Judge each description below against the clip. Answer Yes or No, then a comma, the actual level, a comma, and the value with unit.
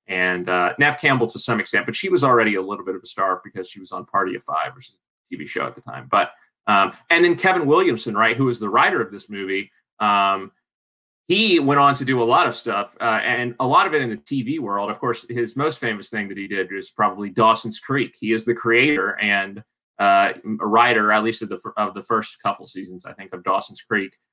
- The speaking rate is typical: No, fast, 250 wpm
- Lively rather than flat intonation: No, average, 3.6 semitones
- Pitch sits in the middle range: No, low, 115 Hz